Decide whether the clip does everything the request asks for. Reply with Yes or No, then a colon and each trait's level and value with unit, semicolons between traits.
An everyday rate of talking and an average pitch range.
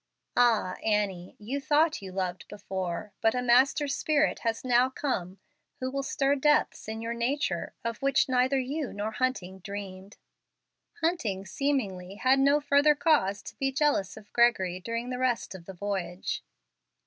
No: average, 160 wpm; wide, 5.9 semitones